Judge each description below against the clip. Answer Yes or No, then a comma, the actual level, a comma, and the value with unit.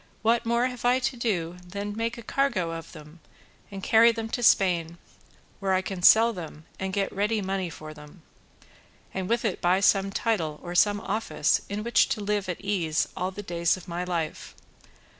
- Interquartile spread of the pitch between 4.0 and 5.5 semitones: Yes, average, 4.3 semitones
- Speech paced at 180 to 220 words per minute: Yes, average, 195 wpm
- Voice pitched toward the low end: No, high, 195 Hz